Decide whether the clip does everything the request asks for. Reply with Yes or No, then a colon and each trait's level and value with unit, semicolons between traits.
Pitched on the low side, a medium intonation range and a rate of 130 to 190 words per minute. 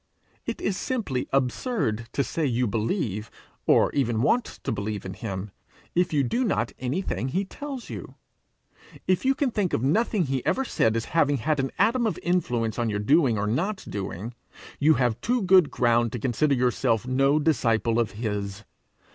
No: low, 130 Hz; wide, 8.2 semitones; average, 180 wpm